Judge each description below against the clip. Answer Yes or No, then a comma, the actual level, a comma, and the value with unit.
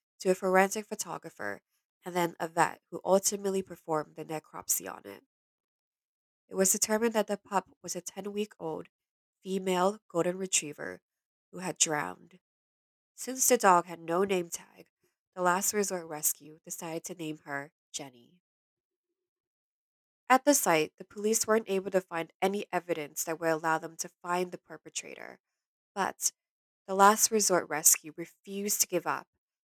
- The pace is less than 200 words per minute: Yes, average, 155 wpm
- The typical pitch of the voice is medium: Yes, medium, 180 Hz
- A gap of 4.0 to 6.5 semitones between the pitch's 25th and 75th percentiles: No, average, 3.6 semitones